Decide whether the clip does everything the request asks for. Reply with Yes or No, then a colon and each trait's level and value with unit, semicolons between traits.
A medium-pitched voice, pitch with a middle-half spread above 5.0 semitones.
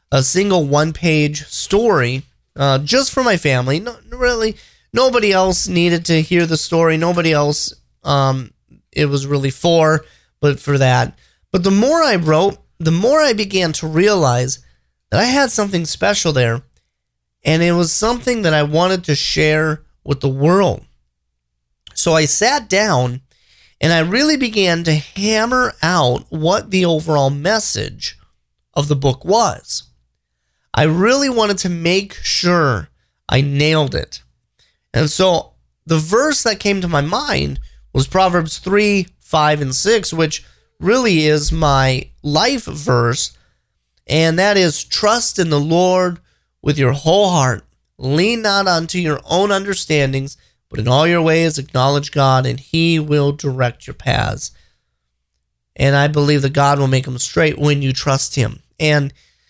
Yes: medium, 155 Hz; wide, 5.4 semitones